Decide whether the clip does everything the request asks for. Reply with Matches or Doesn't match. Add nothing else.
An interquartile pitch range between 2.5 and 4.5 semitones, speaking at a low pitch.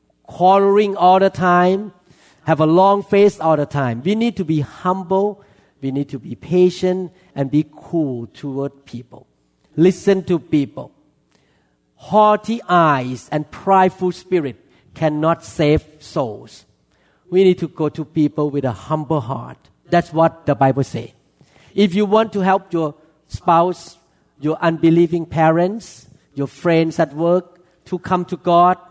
Doesn't match